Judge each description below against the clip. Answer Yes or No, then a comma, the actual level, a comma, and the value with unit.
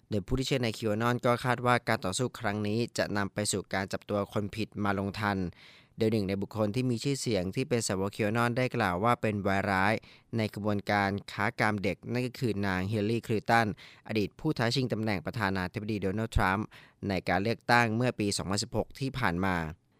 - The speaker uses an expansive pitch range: No, average, 2.9 semitones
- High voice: No, low, 105 Hz